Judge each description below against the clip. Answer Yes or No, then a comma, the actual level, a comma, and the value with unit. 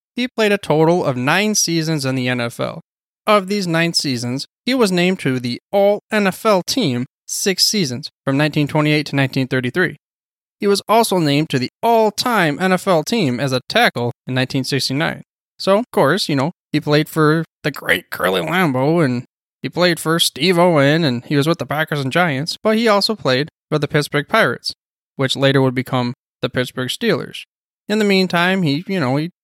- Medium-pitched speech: Yes, medium, 155 Hz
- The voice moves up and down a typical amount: No, wide, 5.8 semitones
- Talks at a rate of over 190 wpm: No, average, 185 wpm